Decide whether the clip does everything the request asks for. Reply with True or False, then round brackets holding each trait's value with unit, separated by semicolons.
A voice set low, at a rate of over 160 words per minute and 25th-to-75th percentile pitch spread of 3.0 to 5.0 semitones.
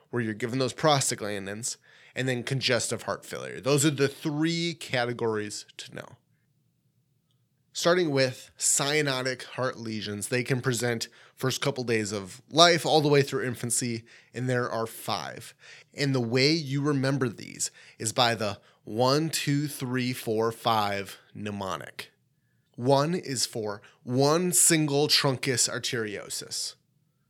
False (130 Hz; 135 wpm; 3.3 semitones)